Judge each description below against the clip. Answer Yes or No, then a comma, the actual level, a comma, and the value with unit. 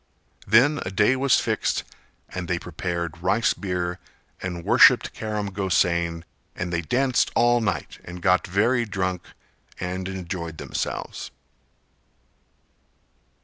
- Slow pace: Yes, slow, 115 wpm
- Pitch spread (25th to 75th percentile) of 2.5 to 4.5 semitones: Yes, average, 3.5 semitones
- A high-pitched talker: No, very low, 95 Hz